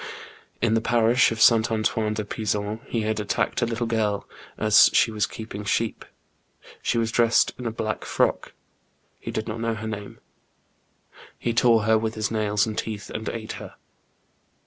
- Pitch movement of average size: No, narrow, 1.2 semitones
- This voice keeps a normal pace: Yes, average, 175 wpm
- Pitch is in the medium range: No, low, 110 Hz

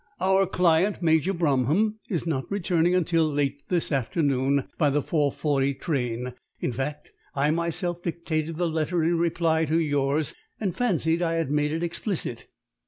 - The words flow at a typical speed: Yes, average, 160 wpm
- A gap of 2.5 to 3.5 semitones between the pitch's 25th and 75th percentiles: Yes, average, 3.2 semitones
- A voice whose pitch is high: No, medium, 160 Hz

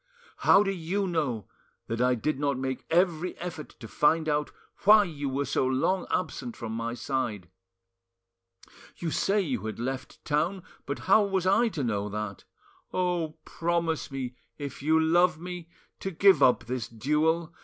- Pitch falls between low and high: Yes, medium, 155 Hz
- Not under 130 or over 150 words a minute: No, average, 165 wpm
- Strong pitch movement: Yes, wide, 5.7 semitones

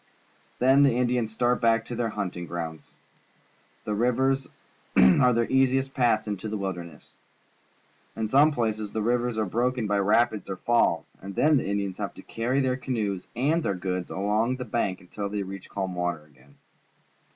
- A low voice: Yes, low, 110 Hz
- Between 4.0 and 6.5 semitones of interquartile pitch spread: Yes, average, 4.3 semitones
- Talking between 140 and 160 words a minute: No, average, 175 wpm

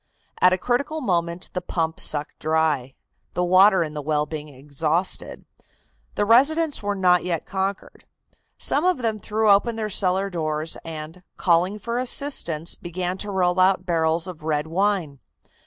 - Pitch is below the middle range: No, medium, 180 Hz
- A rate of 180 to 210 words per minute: No, average, 155 wpm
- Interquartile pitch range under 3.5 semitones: No, average, 4.2 semitones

